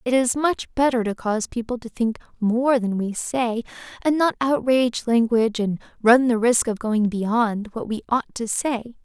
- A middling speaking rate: Yes, average, 190 wpm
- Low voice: No, high, 235 Hz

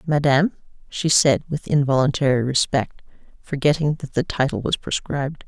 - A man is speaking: No, female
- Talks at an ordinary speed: No, slow, 130 wpm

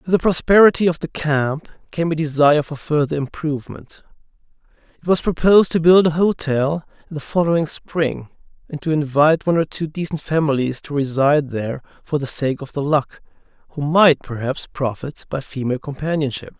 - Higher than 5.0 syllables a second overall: Yes, 5.5 syllables/s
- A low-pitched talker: No, medium, 150 Hz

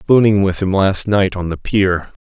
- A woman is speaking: No, male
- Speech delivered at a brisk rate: Yes, fast, 215 wpm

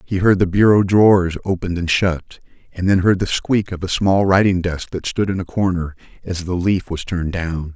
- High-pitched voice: No, very low, 90 Hz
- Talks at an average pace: No, fast, 225 wpm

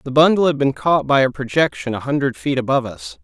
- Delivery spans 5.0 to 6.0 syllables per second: No, 6.2 syllables/s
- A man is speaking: Yes, male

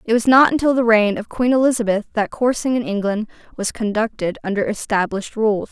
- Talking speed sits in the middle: Yes, average, 190 wpm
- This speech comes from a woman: Yes, female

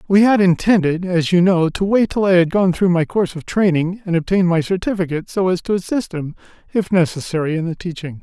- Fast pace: Yes, fast, 225 wpm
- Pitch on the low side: No, medium, 180 Hz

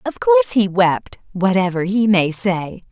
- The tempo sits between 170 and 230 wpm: No, average, 145 wpm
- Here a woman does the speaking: Yes, female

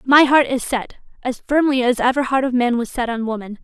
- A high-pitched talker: Yes, very high, 250 Hz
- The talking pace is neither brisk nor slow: No, fast, 250 wpm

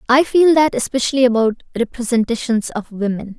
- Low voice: No, high, 240 Hz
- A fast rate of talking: No, average, 140 wpm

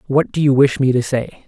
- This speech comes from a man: Yes, male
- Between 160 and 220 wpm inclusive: No, fast, 285 wpm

